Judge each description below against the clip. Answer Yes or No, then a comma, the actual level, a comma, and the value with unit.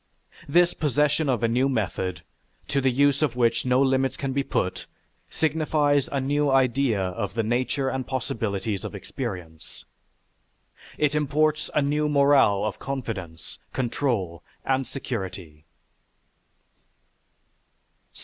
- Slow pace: Yes, slow, 120 wpm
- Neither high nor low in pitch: No, low, 130 Hz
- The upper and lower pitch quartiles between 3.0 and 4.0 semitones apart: No, average, 4.8 semitones